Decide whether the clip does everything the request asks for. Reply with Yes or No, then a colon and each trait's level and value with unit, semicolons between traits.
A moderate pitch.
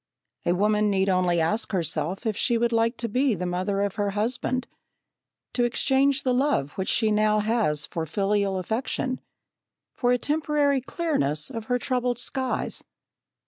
No: high, 220 Hz